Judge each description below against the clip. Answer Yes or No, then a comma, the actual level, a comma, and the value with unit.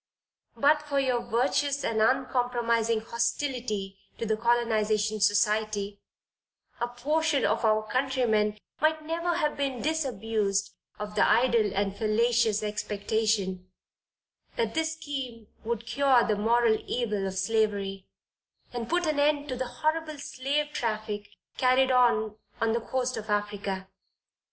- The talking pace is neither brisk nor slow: No, slow, 130 wpm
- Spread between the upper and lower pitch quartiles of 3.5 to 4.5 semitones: Yes, average, 3.8 semitones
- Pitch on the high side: Yes, high, 235 Hz